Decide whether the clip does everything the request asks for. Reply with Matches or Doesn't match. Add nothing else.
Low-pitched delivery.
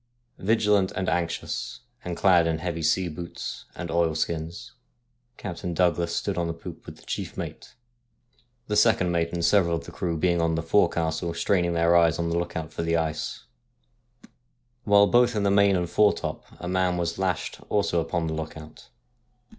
Matches